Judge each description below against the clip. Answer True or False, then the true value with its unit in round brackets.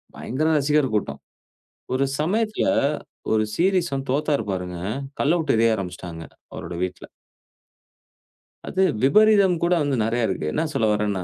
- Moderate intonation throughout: False (8.9 semitones)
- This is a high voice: False (135 Hz)